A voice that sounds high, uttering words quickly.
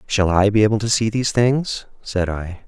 No: low, 105 Hz; fast, 225 wpm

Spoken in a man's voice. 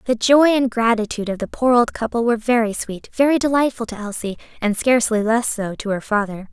No: female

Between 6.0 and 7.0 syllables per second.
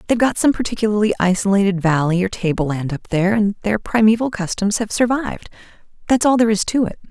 Yes: 6.4 syllables/s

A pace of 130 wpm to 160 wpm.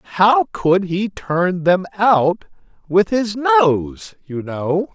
Yes: slow, 135 wpm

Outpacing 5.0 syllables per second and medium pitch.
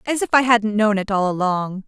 No: 5.2 syllables/s; high, 215 Hz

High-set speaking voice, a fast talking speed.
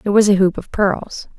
Yes: high, 200 Hz; fast, 260 wpm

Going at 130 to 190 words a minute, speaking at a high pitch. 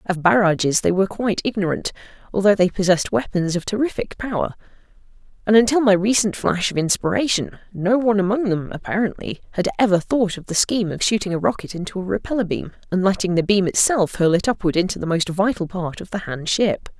No: average, 200 wpm; high, 195 Hz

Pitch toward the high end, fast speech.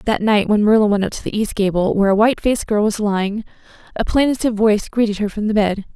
Yes: high, 210 Hz; fast, 250 wpm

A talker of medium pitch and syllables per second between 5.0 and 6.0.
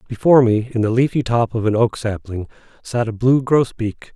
No: low, 115 Hz; 5.3 syllables/s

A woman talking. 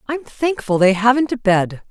Yes: female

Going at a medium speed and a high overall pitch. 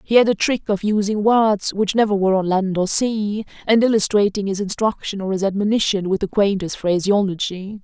Yes: average, 190 wpm; high, 205 Hz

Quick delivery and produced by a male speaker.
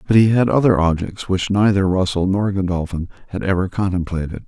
No: average, 175 wpm; male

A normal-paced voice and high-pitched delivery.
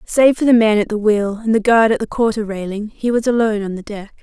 No: fast, 285 wpm; high, 215 Hz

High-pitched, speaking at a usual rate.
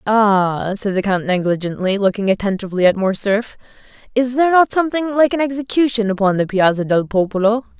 Yes: high, 215 Hz; average, 160 wpm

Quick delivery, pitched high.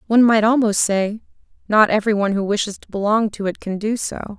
Yes: fast, 220 wpm; high, 210 Hz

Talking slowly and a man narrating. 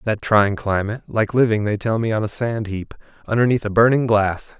No: average, 195 wpm; male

